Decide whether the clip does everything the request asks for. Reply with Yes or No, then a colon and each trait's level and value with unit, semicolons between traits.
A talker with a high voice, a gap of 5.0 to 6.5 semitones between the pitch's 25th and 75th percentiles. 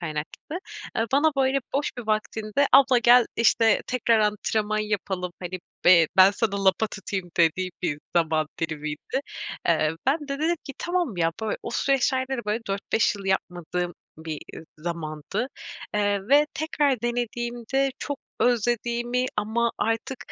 Yes: high, 220 Hz; wide, 5.6 semitones